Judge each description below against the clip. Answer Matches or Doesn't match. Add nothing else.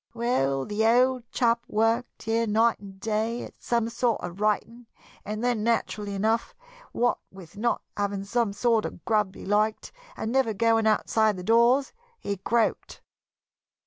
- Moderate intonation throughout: Doesn't match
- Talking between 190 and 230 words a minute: Doesn't match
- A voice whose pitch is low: Doesn't match